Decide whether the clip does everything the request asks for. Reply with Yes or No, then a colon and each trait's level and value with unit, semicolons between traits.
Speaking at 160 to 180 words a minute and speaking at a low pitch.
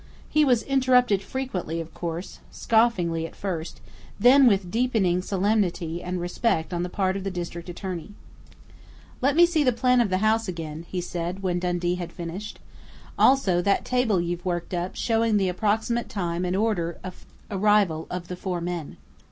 No: average, 170 wpm; medium, 185 Hz